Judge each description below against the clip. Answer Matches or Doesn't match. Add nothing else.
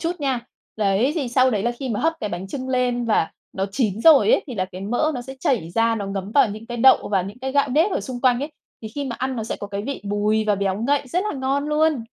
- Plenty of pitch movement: Doesn't match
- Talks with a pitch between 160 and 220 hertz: Doesn't match